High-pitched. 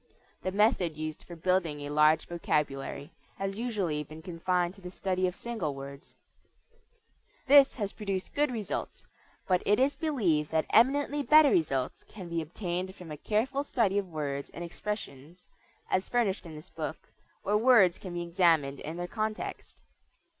No: medium, 180 Hz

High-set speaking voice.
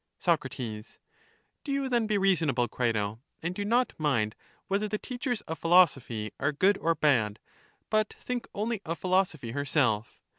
No: medium, 165 Hz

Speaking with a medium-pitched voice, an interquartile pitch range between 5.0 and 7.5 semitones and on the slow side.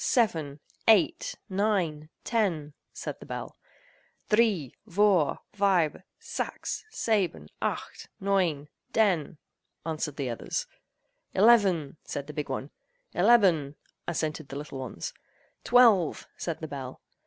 Yes: medium, 165 Hz; wide, 5.6 semitones; slow, 110 wpm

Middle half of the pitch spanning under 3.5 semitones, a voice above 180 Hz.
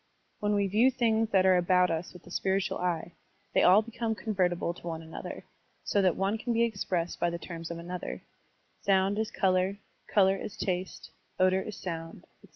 Yes: average, 2.8 semitones; high, 190 Hz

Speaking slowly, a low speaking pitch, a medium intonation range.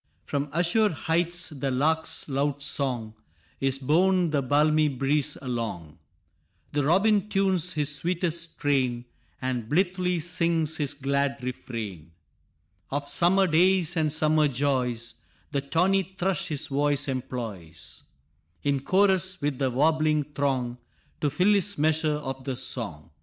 No: slow, 130 wpm; medium, 145 Hz; average, 4.4 semitones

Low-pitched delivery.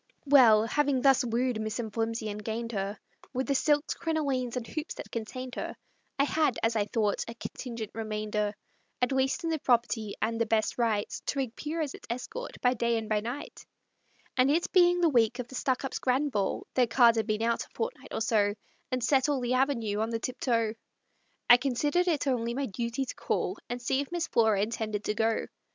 No: high, 240 Hz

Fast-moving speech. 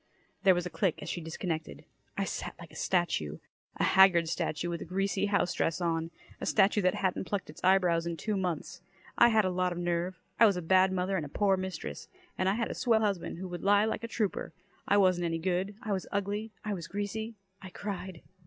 Yes: fast, 225 wpm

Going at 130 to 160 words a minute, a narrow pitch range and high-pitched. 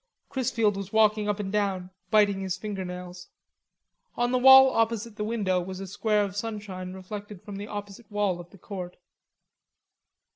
No: average, 170 wpm; narrow, 2.3 semitones; high, 205 Hz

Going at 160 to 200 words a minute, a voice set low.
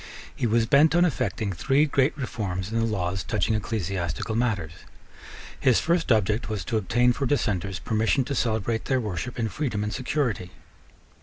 Yes: average, 165 wpm; low, 110 Hz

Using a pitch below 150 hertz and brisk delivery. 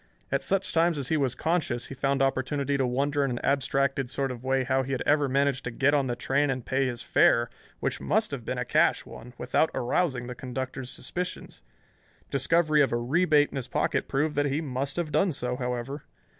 Yes: low, 135 Hz; fast, 215 wpm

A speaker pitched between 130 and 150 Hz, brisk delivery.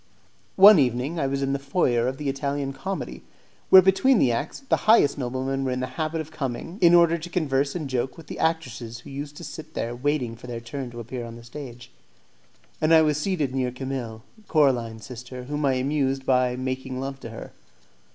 Yes: low, 135 Hz; fast, 210 wpm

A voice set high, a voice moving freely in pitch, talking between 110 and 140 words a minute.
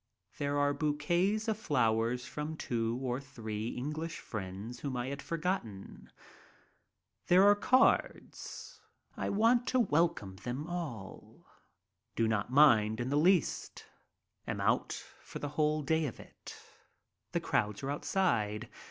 No: medium, 140 Hz; wide, 6.5 semitones; slow, 135 wpm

